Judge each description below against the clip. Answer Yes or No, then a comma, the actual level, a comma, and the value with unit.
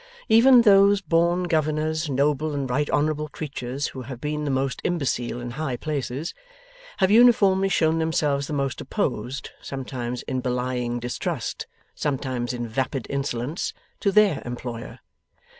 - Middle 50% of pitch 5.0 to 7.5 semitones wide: No, average, 4.3 semitones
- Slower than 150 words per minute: Yes, average, 140 wpm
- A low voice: No, medium, 145 Hz